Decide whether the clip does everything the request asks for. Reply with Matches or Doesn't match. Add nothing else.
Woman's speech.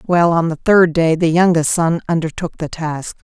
Matches